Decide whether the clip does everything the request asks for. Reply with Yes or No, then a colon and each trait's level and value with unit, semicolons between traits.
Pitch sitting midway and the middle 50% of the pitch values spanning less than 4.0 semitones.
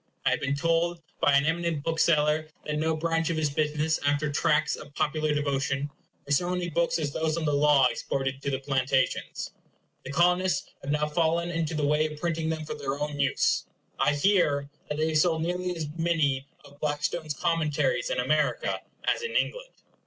Yes: medium, 155 Hz; narrow, 2.6 semitones